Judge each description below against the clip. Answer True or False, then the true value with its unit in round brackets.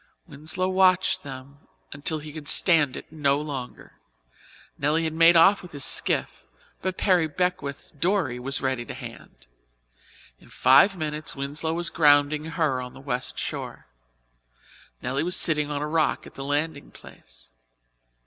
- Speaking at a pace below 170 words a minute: True (150 wpm)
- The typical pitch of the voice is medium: True (150 Hz)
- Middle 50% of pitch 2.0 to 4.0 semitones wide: True (3.0 semitones)